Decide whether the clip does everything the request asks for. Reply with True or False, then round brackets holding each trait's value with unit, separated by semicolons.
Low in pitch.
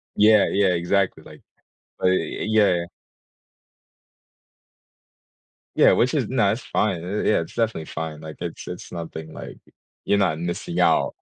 True (95 Hz)